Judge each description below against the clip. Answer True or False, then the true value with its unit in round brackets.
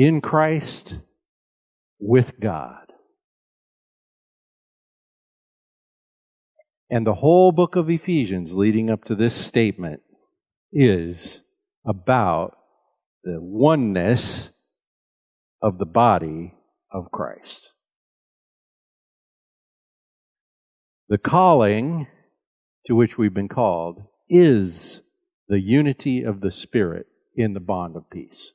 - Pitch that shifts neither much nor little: False (8.0 semitones)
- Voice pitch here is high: False (115 Hz)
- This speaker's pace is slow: True (90 wpm)